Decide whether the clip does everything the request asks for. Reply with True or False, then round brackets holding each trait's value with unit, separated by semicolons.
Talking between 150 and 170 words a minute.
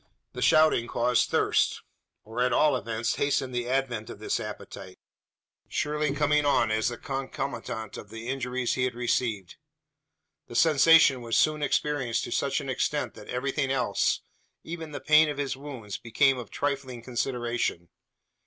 True (155 wpm)